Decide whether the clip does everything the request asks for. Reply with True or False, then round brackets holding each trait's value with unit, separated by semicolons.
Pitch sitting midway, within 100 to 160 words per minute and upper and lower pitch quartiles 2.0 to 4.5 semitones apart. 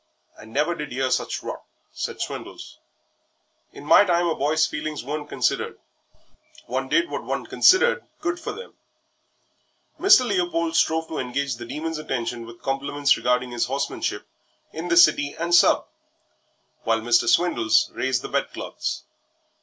False (150 Hz; 145 wpm; 5.4 semitones)